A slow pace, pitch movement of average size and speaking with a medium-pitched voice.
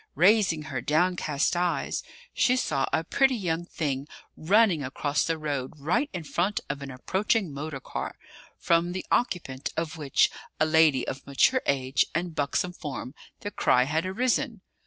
No: average, 155 wpm; average, 4.7 semitones; medium, 160 Hz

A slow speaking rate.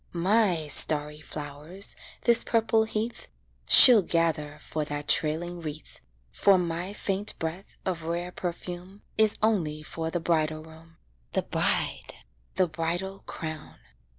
Yes: slow, 125 wpm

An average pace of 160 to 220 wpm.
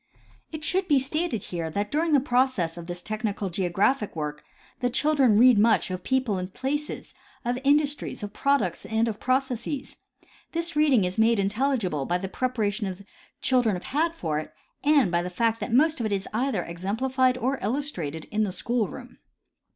Yes: average, 190 wpm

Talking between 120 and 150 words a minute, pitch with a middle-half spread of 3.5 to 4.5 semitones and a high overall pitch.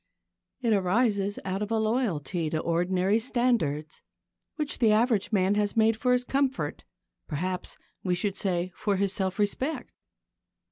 Yes: average, 145 wpm; average, 3.9 semitones; high, 205 Hz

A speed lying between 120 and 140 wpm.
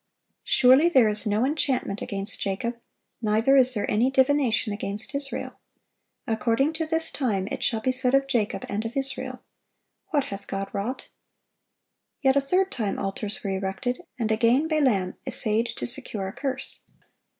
No: average, 160 wpm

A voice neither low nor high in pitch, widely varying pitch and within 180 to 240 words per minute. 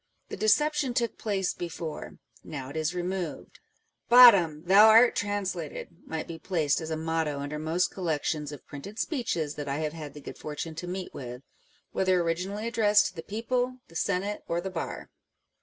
No: medium, 175 Hz; average, 4.8 semitones; average, 190 wpm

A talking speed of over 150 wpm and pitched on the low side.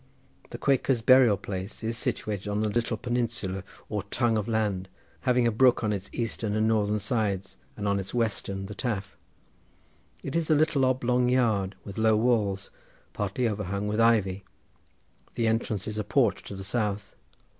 Yes: average, 170 wpm; low, 110 Hz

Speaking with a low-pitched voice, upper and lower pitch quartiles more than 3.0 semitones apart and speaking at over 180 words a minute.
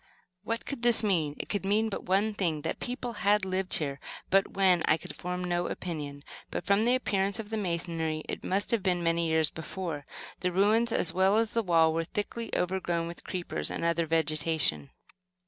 No: medium, 180 Hz; average, 4.0 semitones; average, 200 wpm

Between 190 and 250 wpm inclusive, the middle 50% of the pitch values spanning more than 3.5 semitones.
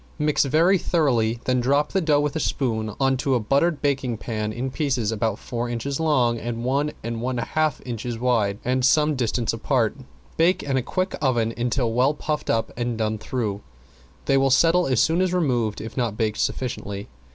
Yes: average, 195 wpm; average, 4.1 semitones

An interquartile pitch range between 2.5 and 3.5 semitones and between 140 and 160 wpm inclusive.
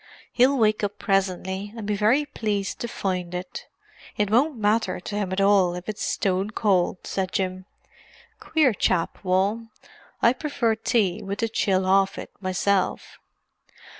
Yes: average, 2.8 semitones; average, 155 wpm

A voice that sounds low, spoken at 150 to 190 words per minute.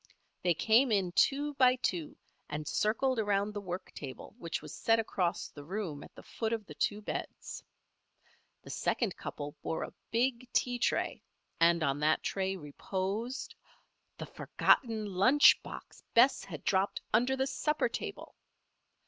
No: high, 205 Hz; average, 155 wpm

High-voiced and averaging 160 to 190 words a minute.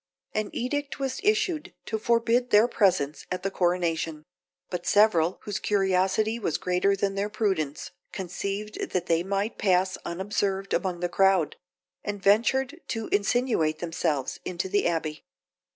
No: high, 195 Hz; average, 140 wpm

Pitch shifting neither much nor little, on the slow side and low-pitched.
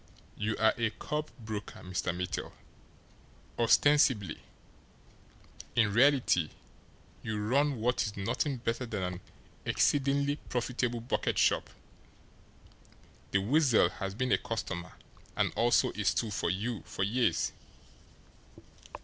Yes: average, 4.2 semitones; slow, 115 wpm; low, 115 Hz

